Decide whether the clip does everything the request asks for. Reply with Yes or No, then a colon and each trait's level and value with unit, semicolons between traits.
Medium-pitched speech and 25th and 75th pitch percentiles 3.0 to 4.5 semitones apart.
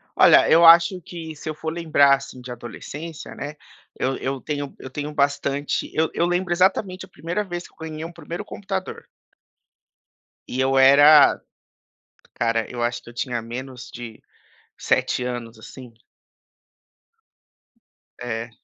No: medium, 145 Hz; average, 5.1 semitones